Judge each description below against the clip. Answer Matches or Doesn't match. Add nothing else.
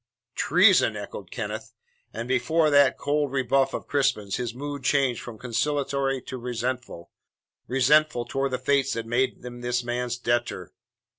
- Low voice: Matches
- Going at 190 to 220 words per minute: Doesn't match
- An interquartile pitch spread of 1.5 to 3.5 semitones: Matches